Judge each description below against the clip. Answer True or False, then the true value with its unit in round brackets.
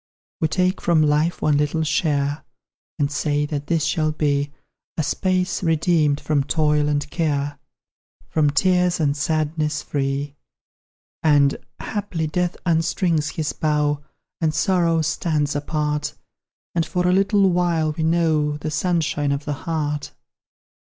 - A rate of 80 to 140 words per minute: True (135 wpm)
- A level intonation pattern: True (2.2 semitones)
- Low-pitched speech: False (155 Hz)